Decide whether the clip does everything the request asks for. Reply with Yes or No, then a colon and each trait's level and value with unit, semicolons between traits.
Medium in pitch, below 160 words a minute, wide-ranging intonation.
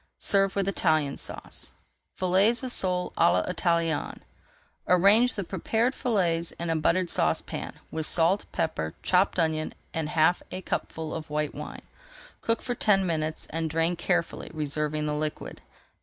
No: medium, 170 Hz; average, 145 wpm; average, 3.6 semitones